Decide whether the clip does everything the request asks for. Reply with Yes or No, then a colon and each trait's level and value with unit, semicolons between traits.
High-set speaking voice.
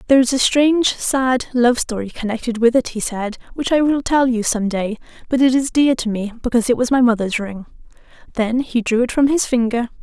Yes: high, 240 Hz